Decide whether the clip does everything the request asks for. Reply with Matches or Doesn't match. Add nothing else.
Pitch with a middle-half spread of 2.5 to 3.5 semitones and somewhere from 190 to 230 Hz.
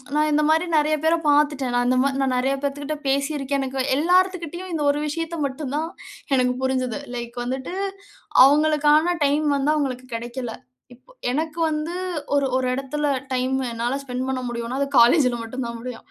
Doesn't match